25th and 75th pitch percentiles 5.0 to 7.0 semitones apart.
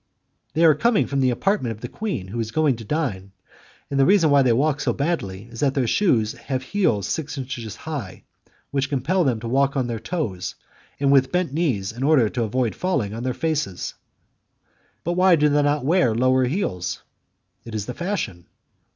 Yes: wide, 5.5 semitones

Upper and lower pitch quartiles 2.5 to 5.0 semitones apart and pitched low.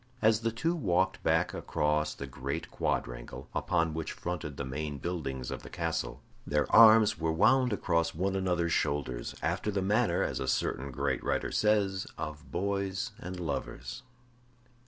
No: wide, 5.4 semitones; very low, 85 Hz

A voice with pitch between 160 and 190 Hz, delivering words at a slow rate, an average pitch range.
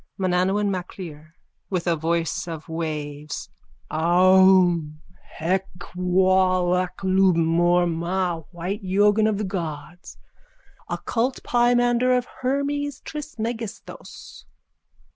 Yes: medium, 185 Hz; slow, 100 wpm; average, 3.5 semitones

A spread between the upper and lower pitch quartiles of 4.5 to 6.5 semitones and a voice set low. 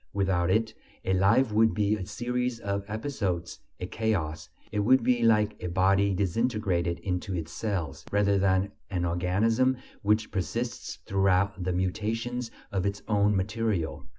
No: average, 3.3 semitones; low, 100 Hz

